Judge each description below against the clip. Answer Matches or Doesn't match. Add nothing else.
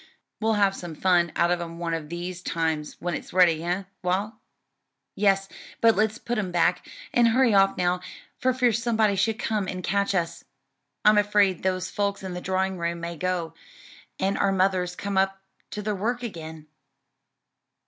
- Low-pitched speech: Doesn't match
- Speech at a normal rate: Matches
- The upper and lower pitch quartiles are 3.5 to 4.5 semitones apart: Doesn't match